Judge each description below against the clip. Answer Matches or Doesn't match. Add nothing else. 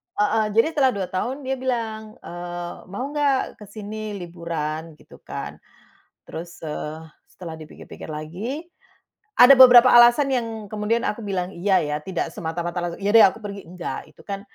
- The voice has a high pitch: Matches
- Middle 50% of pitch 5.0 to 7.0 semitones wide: Matches